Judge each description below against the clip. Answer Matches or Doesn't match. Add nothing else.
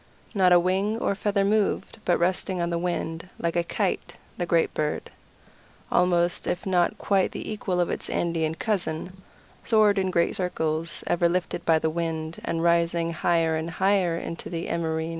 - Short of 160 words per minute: Doesn't match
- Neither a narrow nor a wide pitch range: Doesn't match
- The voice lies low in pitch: Doesn't match